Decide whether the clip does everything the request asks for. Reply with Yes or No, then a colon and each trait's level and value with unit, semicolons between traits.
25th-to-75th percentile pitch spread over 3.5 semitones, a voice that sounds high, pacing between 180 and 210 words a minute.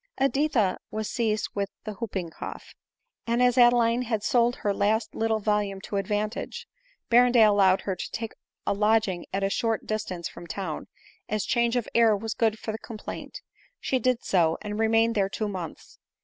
No: narrow, 2.6 semitones; high, 215 Hz; average, 185 wpm